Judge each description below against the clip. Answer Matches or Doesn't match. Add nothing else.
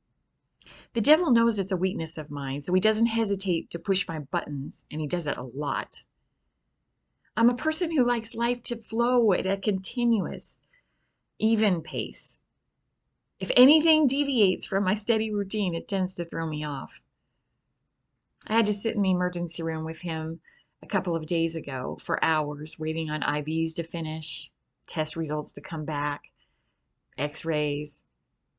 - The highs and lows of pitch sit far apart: Matches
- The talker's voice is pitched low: Doesn't match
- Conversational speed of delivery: Matches